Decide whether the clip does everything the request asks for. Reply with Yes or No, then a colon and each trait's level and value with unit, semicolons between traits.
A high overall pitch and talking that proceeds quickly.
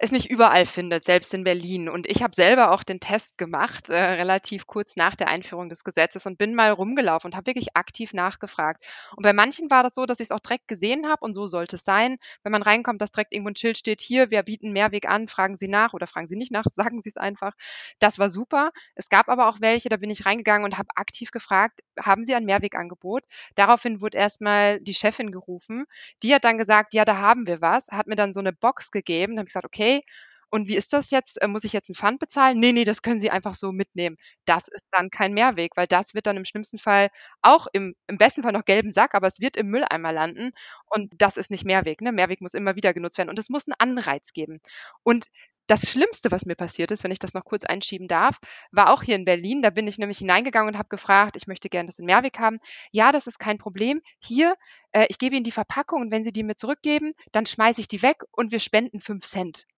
Yes: high, 210 Hz; fast, 250 wpm